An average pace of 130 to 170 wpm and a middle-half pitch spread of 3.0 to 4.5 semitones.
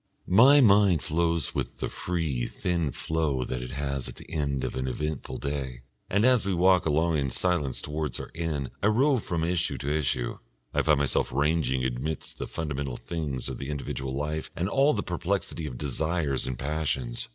No: average, 185 wpm; average, 4.2 semitones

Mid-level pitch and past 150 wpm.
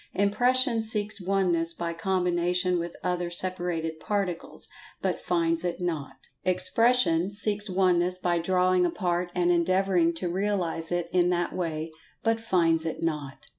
No: medium, 180 Hz; average, 140 wpm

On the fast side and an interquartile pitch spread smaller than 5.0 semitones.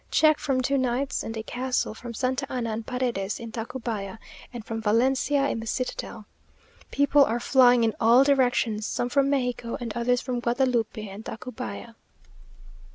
No: average, 160 wpm; narrow, 2.6 semitones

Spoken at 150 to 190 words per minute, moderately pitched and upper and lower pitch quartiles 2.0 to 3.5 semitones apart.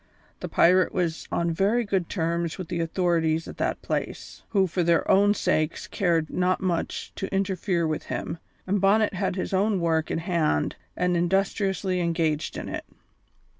Yes: average, 170 wpm; medium, 180 Hz; narrow, 2.6 semitones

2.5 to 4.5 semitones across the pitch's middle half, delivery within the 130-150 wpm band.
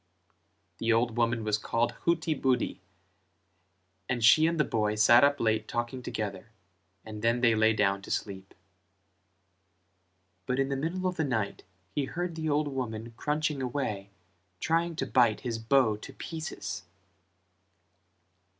No: average, 4.9 semitones; average, 140 wpm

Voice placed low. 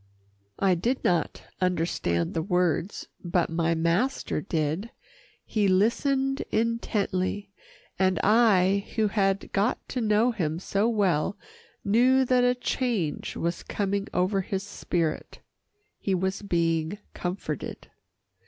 No: high, 195 Hz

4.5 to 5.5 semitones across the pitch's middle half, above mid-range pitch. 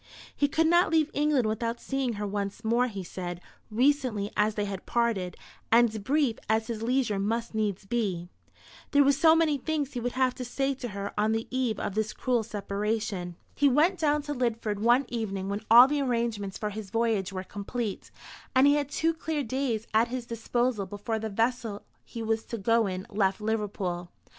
No: average, 4.0 semitones; high, 230 Hz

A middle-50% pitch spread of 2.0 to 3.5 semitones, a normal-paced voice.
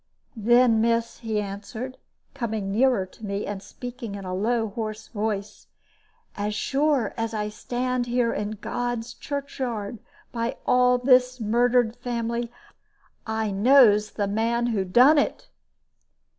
No: average, 2.8 semitones; slow, 130 wpm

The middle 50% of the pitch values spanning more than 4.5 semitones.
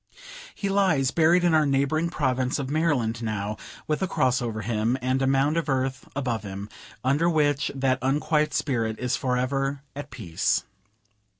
No: average, 3.5 semitones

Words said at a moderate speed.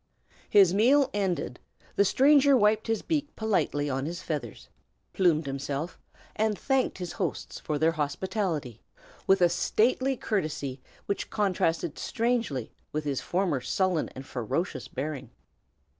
No: slow, 130 wpm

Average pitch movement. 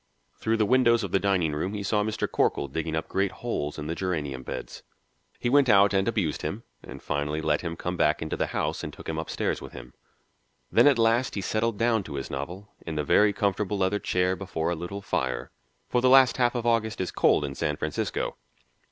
No: wide, 5.8 semitones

